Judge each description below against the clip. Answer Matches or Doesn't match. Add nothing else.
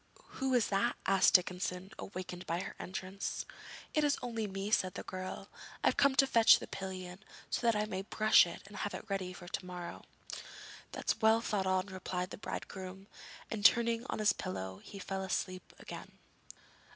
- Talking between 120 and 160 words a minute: Doesn't match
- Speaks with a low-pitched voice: Doesn't match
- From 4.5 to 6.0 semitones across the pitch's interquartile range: Doesn't match